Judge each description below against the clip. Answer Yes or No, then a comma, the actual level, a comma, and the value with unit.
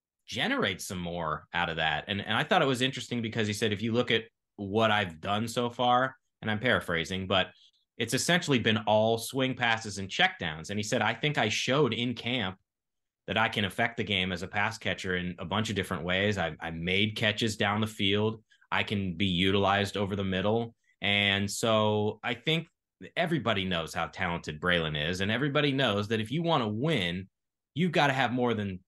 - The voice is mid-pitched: No, low, 105 Hz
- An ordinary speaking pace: No, fast, 210 wpm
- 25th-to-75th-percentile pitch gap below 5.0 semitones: Yes, average, 3.8 semitones